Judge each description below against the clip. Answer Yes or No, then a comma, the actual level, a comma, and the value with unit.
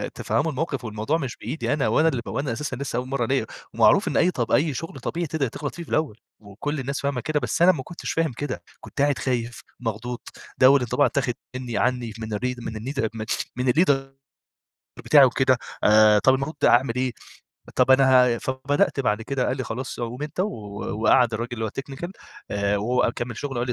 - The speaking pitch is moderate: No, low, 130 Hz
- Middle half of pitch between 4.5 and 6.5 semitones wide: No, average, 3.0 semitones